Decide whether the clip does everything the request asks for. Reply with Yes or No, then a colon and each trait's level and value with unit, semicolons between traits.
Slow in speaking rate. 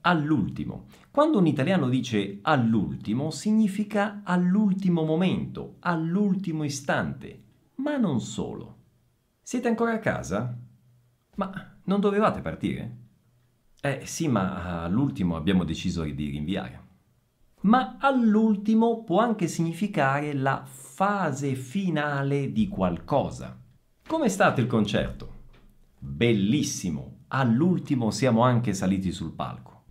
Yes: slow, 105 wpm